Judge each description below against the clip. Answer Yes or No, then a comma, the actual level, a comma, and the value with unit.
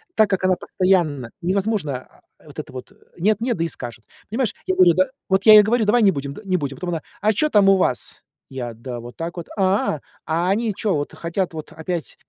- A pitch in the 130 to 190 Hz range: Yes, medium, 185 Hz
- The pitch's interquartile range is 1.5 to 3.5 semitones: No, average, 5.2 semitones